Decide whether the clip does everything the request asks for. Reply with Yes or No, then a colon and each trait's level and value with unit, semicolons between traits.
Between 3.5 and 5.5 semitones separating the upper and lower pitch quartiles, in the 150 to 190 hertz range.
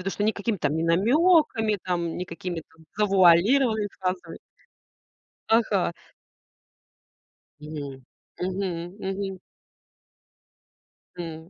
Yes: average, 3.9 semitones; medium, 185 Hz